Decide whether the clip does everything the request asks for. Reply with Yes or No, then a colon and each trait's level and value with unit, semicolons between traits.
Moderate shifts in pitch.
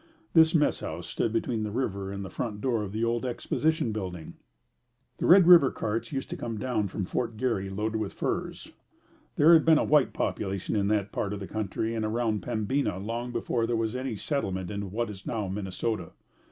Yes: average, 3.7 semitones